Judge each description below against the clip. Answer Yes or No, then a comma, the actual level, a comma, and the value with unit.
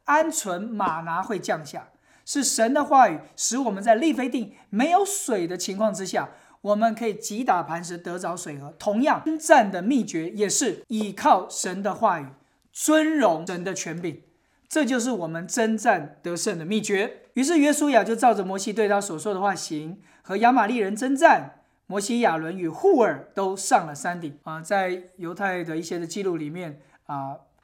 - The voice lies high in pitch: Yes, high, 205 Hz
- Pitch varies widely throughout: Yes, wide, 6.2 semitones